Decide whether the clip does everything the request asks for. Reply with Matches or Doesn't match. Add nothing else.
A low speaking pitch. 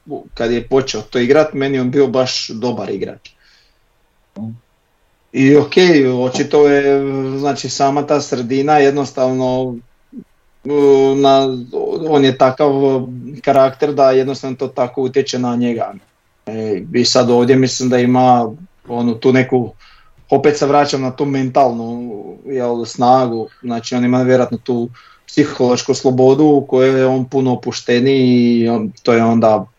Matches